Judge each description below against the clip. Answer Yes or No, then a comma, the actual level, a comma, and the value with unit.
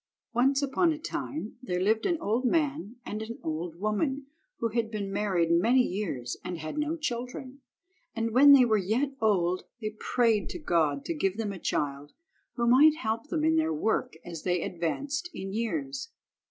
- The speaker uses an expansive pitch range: Yes, wide, 6.8 semitones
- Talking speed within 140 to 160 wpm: No, average, 180 wpm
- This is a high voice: Yes, high, 225 Hz